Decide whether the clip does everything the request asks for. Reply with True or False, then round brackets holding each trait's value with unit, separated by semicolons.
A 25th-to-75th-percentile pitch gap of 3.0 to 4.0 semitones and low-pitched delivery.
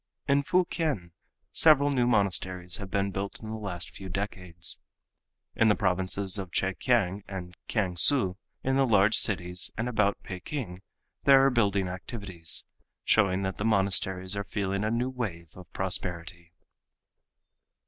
True (3.6 semitones; 100 Hz)